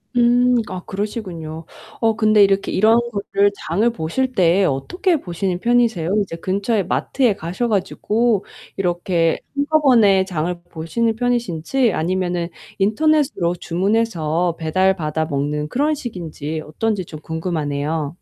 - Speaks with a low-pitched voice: No, high, 190 Hz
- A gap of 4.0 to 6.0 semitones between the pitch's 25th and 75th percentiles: Yes, wide, 5.6 semitones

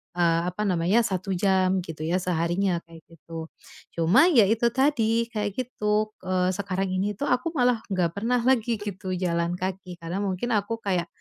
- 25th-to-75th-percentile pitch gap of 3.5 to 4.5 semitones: Yes, average, 4.1 semitones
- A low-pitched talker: No, high, 190 Hz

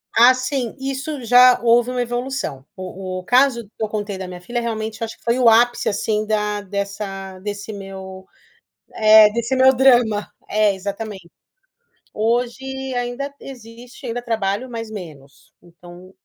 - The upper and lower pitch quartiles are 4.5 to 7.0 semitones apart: No, average, 3.8 semitones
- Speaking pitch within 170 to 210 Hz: No, high, 220 Hz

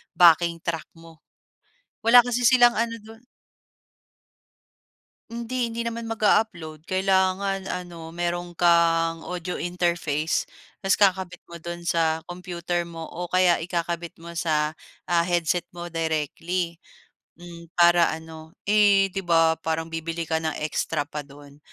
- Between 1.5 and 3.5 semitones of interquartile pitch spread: Yes, narrow, 2.4 semitones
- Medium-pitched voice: Yes, medium, 175 Hz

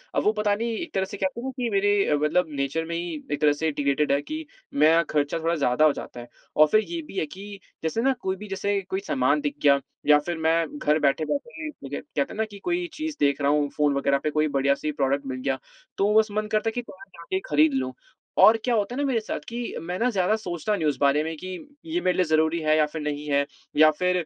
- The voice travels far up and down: Yes, wide, 6.1 semitones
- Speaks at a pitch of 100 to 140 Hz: No, medium, 165 Hz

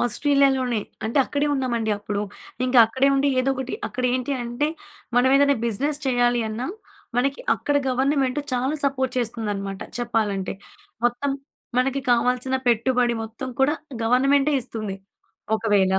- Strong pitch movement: No, average, 2.9 semitones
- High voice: Yes, very high, 250 Hz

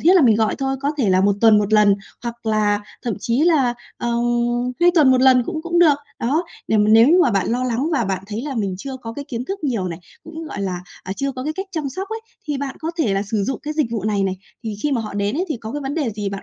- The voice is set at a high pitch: Yes, high, 240 Hz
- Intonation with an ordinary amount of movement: No, wide, 5.8 semitones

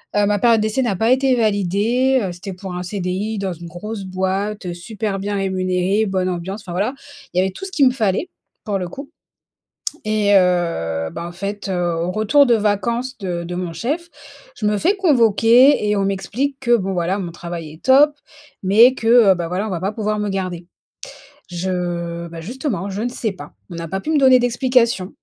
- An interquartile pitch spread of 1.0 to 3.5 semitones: No, average, 4.3 semitones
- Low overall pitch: No, high, 200 Hz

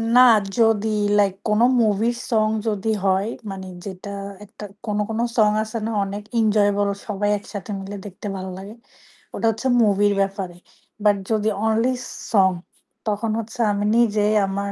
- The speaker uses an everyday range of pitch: No, narrow, 1.7 semitones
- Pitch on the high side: Yes, high, 210 Hz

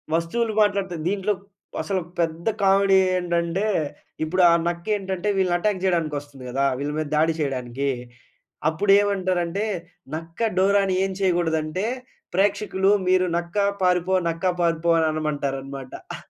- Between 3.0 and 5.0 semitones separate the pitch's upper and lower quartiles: Yes, average, 3.4 semitones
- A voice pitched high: No, medium, 175 Hz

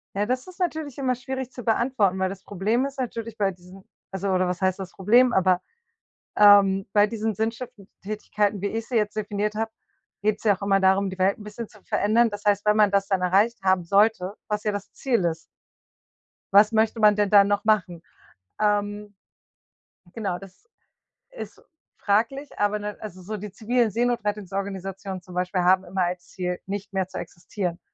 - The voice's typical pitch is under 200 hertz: No, high, 205 Hz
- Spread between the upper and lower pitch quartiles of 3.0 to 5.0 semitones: No, narrow, 2.5 semitones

